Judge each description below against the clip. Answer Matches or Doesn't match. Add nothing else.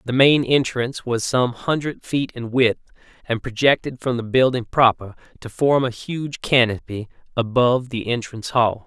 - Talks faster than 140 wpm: Matches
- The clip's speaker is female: Doesn't match